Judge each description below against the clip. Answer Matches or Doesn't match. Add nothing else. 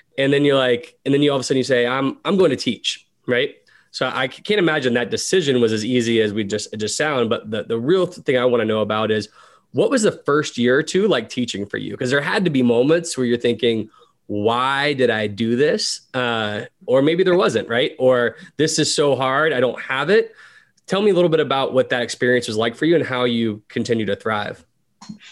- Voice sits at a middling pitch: Doesn't match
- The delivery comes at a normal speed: Doesn't match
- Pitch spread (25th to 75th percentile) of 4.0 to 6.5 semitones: Matches